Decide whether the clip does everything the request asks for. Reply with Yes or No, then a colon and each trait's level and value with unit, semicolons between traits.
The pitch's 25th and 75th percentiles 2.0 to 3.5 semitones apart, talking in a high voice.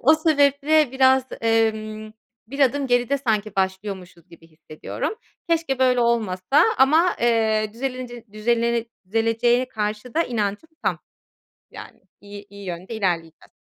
No: average, 4.2 semitones; high, 230 Hz